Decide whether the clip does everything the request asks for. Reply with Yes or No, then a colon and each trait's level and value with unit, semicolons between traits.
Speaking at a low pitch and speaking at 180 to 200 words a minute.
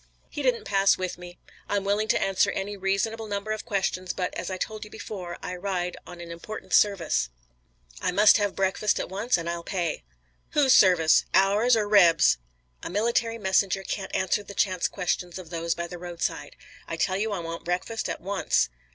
No: high, 195 Hz; average, 195 wpm